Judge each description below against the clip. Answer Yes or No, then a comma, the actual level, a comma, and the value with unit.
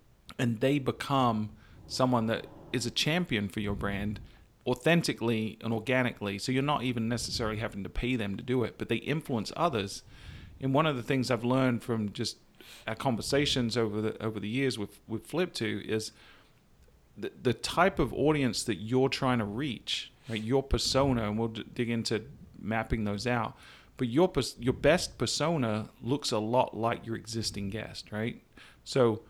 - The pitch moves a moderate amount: Yes, average, 3.1 semitones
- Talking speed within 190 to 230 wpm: No, average, 180 wpm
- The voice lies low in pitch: Yes, low, 115 Hz